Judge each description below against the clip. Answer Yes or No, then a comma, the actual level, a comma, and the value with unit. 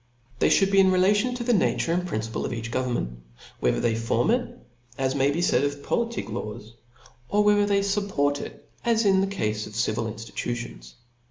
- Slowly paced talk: No, average, 190 wpm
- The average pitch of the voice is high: No, medium, 145 Hz